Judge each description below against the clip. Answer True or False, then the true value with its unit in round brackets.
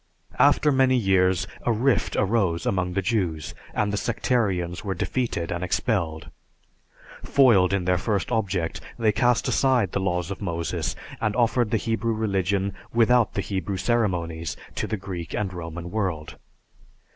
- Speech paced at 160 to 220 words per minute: False (150 wpm)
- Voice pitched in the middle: False (100 Hz)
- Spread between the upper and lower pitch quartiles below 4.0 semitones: False (4.3 semitones)